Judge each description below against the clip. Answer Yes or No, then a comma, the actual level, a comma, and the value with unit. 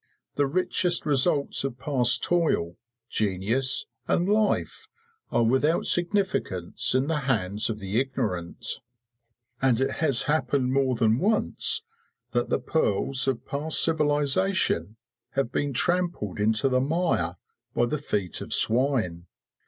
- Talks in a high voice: No, low, 135 Hz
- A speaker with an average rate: No, slow, 130 wpm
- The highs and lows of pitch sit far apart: Yes, wide, 5.9 semitones